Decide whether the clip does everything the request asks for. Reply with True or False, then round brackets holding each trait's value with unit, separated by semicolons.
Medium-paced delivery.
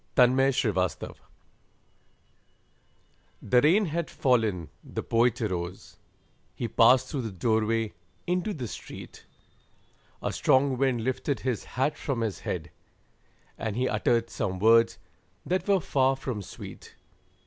False (125 wpm)